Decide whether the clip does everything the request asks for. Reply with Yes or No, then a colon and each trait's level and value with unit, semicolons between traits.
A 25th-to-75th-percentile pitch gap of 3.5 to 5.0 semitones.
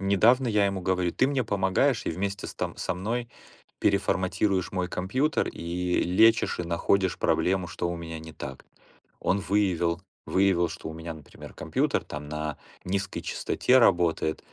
No: average, 2.9 semitones